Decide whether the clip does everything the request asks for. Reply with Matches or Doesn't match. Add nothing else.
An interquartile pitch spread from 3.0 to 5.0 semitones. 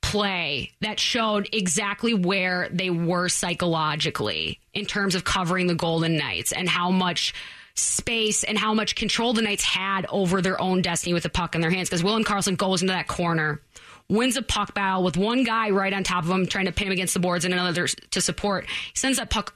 Doesn't match